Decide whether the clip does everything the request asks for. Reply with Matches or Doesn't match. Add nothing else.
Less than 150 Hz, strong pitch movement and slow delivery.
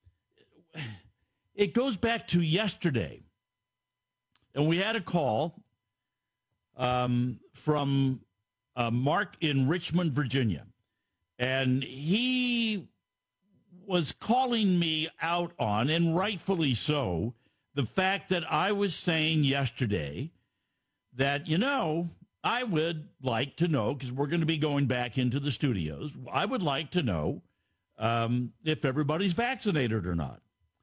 Matches